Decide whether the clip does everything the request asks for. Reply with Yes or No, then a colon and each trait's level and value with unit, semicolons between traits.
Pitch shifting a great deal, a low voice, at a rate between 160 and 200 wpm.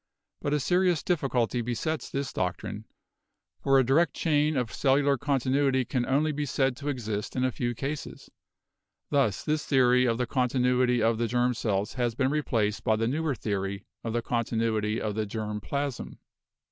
No: average, 3.7 semitones; low, 125 Hz; average, 170 wpm